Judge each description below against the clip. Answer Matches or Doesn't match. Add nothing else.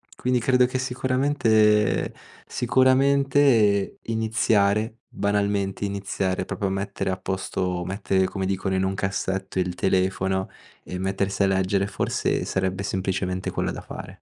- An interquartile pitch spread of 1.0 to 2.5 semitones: Doesn't match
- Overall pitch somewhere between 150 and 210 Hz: Doesn't match